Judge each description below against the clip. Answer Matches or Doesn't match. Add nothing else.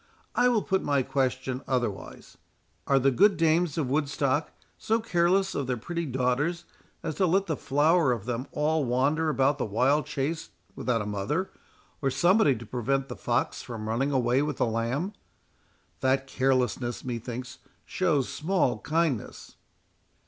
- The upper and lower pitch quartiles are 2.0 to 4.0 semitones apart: Doesn't match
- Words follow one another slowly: Doesn't match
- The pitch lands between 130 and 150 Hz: Matches